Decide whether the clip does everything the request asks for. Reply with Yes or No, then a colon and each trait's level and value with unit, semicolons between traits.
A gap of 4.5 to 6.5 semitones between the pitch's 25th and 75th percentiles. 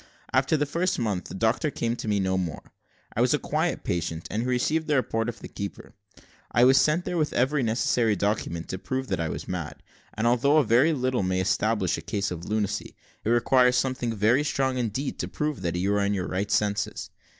Yes: average, 4.8 semitones